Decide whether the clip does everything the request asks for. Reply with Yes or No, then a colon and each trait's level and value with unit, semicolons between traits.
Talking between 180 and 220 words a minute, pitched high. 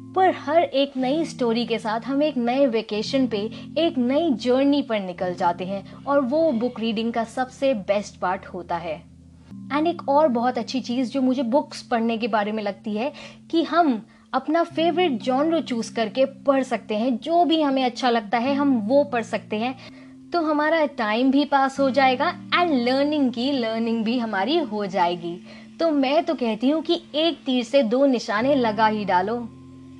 Yes: fast, 190 wpm; very high, 255 Hz